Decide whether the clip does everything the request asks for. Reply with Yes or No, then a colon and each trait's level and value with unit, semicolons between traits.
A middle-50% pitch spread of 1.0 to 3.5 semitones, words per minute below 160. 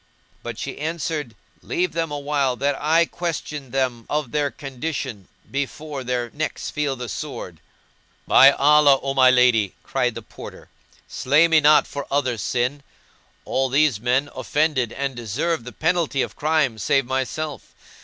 Yes: average, 3.2 semitones; average, 150 wpm